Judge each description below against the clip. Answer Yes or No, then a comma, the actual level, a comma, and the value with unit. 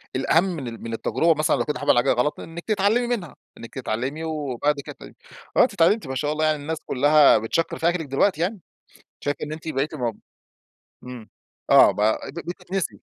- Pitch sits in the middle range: Yes, medium, 150 Hz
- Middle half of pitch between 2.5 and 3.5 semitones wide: No, average, 4.6 semitones